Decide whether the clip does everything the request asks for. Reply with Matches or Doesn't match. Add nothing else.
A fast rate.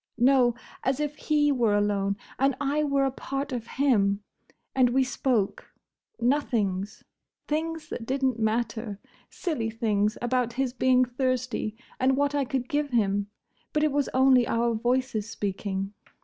Doesn't match